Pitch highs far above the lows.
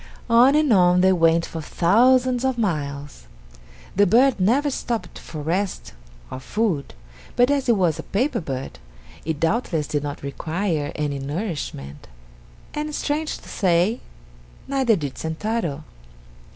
Yes: wide, 7.8 semitones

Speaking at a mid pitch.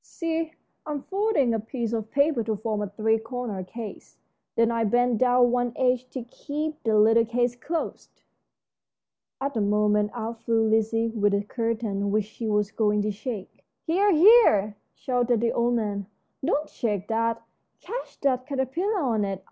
No: high, 230 Hz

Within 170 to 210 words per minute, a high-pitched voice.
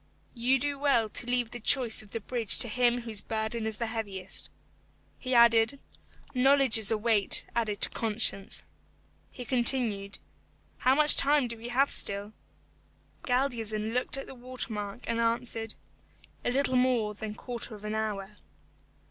No: average, 160 wpm; high, 230 Hz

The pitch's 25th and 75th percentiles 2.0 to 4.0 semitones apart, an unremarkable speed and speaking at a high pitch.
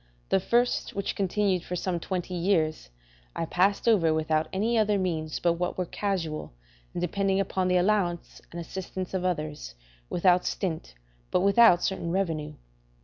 No: average, 2.9 semitones; average, 155 wpm; medium, 180 Hz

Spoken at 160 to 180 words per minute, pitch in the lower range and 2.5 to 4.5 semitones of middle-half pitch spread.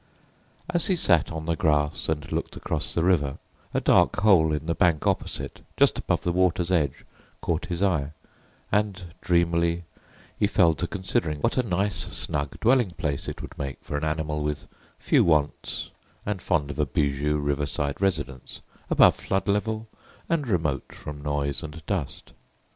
Yes: average, 165 wpm; very low, 80 Hz; average, 3.9 semitones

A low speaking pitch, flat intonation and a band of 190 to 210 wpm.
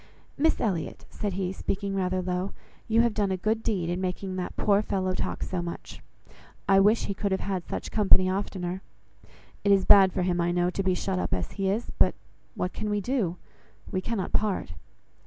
No: high, 190 Hz; narrow, 2.0 semitones; average, 200 wpm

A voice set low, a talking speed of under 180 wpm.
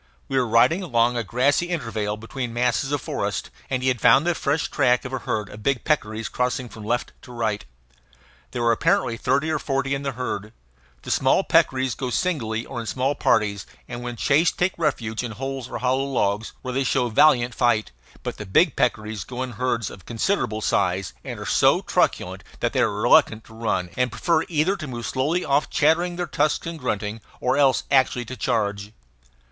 No: low, 125 Hz; average, 200 wpm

